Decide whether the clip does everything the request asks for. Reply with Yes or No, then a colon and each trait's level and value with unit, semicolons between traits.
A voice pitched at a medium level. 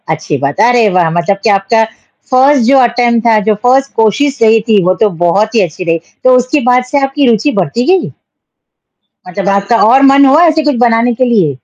No: high, 230 Hz